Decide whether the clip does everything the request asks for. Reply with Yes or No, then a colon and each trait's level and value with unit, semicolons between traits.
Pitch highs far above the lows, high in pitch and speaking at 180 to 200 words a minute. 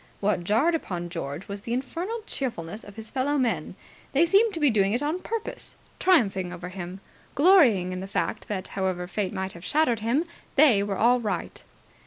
Yes: wide, 7.5 semitones; high, 215 Hz; average, 190 wpm